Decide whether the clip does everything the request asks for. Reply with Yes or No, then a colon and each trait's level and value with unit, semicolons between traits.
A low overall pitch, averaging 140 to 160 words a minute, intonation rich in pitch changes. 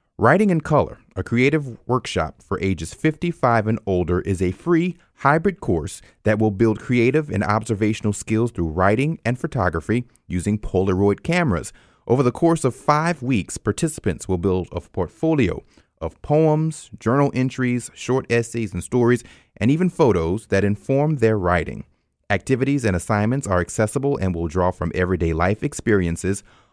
Yes: low, 110 Hz; average, 155 wpm; wide, 6.3 semitones